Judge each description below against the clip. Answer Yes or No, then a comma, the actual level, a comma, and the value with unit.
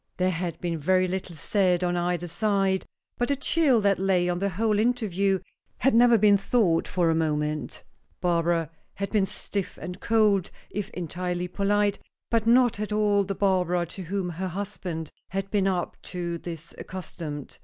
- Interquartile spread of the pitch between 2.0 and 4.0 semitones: Yes, average, 2.8 semitones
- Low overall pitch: No, medium, 185 Hz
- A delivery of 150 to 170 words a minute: Yes, average, 165 wpm